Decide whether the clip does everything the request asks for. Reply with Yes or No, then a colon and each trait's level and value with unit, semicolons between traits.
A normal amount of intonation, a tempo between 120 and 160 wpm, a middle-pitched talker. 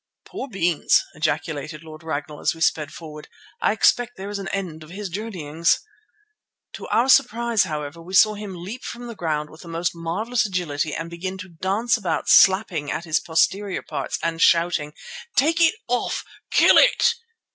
No: average, 4.7 semitones; average, 175 wpm; medium, 175 Hz